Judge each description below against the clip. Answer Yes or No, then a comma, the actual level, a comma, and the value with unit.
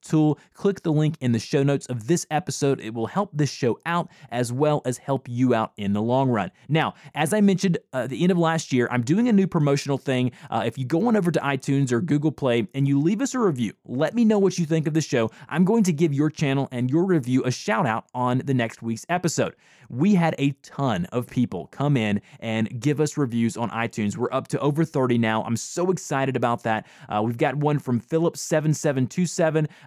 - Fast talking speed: Yes, fast, 235 wpm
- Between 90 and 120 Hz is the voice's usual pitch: No, medium, 140 Hz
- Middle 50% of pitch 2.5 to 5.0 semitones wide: Yes, average, 4.7 semitones